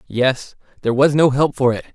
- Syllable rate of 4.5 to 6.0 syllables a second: Yes, 5.5 syllables/s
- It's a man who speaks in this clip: Yes, male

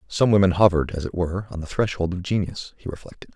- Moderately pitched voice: No, very low, 90 Hz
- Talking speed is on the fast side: Yes, fast, 230 wpm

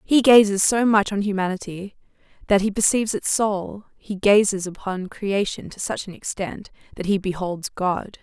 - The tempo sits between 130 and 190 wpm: Yes, average, 170 wpm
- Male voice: No, female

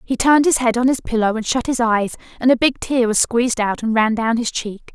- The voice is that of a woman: Yes, female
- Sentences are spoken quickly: Yes, fast, 280 wpm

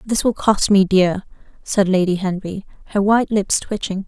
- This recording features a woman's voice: Yes, female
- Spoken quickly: No, average, 175 wpm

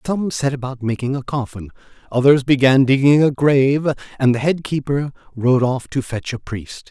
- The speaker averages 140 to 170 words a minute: No, average, 180 wpm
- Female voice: No, male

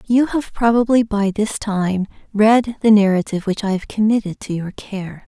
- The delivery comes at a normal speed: Yes, average, 180 wpm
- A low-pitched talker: No, high, 210 Hz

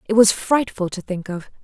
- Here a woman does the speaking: Yes, female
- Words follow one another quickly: Yes, fast, 220 wpm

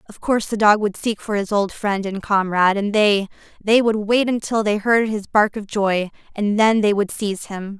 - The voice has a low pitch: No, high, 210 Hz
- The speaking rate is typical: No, fast, 225 wpm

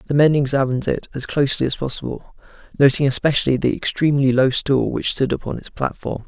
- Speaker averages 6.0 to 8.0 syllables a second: Yes, 6.2 syllables/s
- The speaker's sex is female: No, male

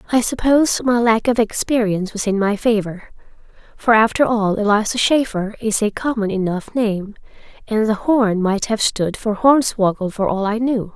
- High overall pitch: Yes, high, 220 Hz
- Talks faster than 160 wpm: Yes, average, 175 wpm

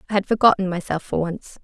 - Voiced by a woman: Yes, female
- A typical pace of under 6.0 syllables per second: No, 6.3 syllables/s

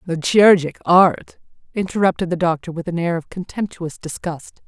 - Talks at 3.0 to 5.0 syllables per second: No, 5.3 syllables/s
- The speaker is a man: No, female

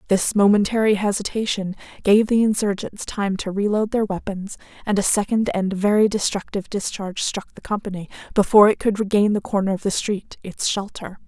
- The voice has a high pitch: Yes, high, 205 Hz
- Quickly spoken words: No, average, 175 wpm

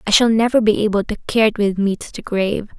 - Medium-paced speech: No, fast, 280 wpm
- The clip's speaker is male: No, female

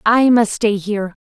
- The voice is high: Yes, high, 215 Hz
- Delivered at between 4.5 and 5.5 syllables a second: Yes, 4.7 syllables/s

